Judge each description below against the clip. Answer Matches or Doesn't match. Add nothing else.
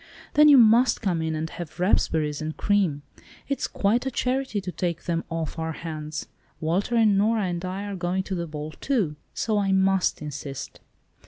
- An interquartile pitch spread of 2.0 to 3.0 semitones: Doesn't match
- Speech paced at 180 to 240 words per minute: Matches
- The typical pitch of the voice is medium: Matches